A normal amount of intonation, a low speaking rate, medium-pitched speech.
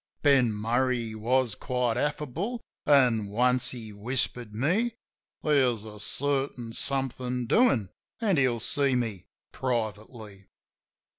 No: average, 3.7 semitones; slow, 105 wpm; low, 125 Hz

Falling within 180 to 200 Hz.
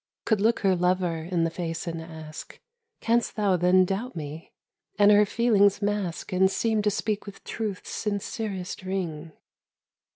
Yes: high, 190 Hz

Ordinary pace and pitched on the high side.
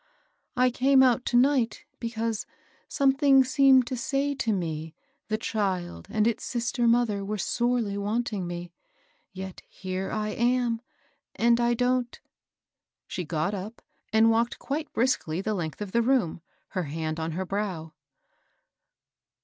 Yes: average, 150 wpm; high, 225 Hz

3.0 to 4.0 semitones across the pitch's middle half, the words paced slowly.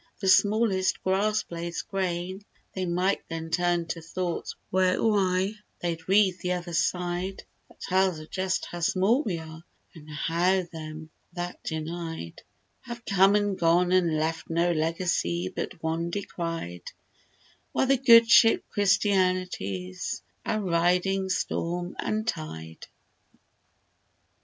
No: narrow, 2.6 semitones; slow, 125 wpm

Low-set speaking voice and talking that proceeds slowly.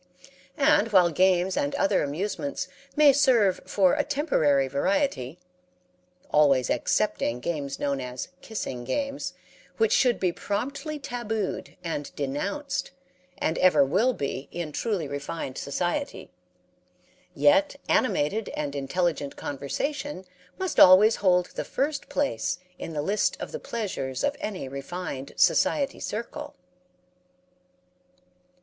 No: medium, 185 Hz; slow, 115 wpm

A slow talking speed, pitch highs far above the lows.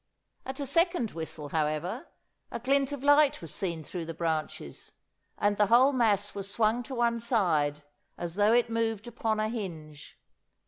No: average, 170 wpm; wide, 6.6 semitones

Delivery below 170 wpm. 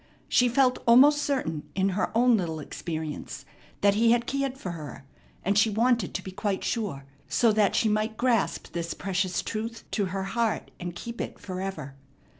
No: average, 180 wpm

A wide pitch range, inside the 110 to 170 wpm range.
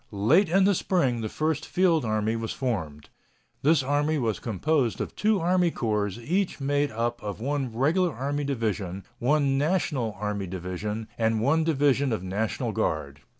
Yes: wide, 6.2 semitones; average, 160 wpm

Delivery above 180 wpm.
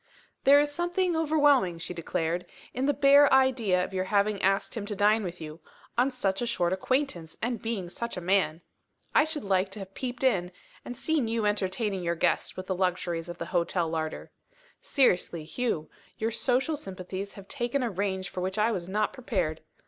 Yes: average, 195 wpm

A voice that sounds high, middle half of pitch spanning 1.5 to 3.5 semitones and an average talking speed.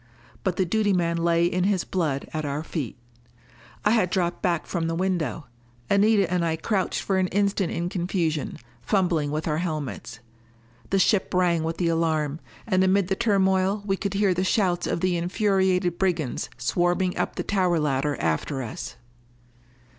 No: medium, 180 Hz; average, 2.9 semitones; average, 170 wpm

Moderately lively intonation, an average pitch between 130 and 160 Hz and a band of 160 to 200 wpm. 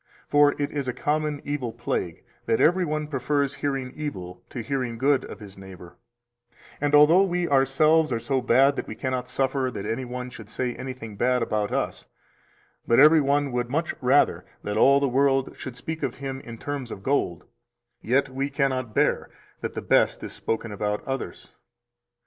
Yes: average, 3.2 semitones; low, 135 Hz; average, 185 wpm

